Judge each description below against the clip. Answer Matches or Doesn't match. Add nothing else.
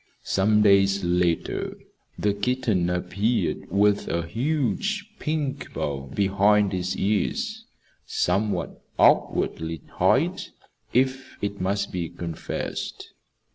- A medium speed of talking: Doesn't match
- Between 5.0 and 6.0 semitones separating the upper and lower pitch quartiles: Matches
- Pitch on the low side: Matches